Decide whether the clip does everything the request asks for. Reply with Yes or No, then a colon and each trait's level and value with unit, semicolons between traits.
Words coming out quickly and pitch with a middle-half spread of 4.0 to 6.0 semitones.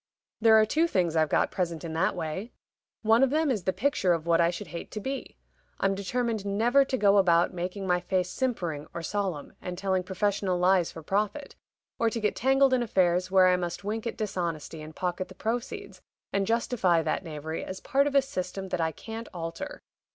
Yes: fast, 210 wpm; average, 4.5 semitones